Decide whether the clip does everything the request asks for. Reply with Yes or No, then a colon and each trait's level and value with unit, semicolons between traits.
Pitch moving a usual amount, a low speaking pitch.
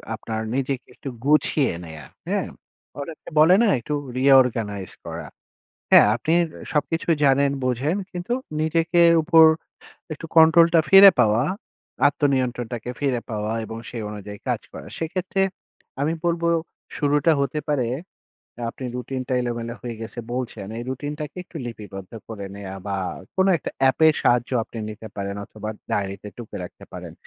No: wide, 5.7 semitones; low, 130 Hz